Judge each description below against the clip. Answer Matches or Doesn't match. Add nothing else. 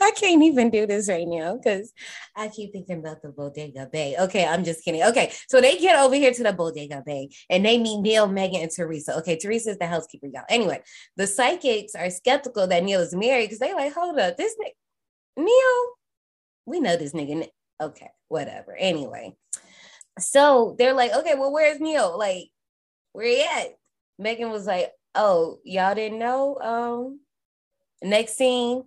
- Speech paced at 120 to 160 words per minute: Doesn't match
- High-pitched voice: Matches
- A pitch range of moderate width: Doesn't match